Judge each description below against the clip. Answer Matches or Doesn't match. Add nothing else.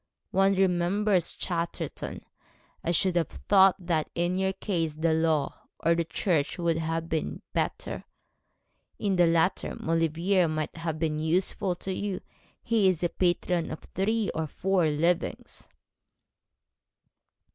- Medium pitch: Matches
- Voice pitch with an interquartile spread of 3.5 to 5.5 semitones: Doesn't match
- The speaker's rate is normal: Doesn't match